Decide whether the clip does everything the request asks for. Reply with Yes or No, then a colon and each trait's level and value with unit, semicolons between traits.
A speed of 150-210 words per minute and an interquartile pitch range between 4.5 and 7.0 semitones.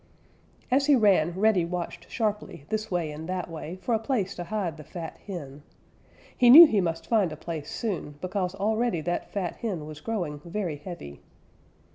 Yes: average, 180 wpm; average, 4.8 semitones